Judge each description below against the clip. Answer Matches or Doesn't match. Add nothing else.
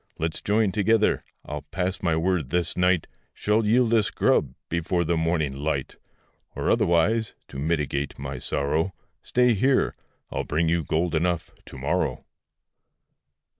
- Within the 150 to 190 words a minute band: Doesn't match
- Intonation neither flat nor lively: Matches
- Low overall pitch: Matches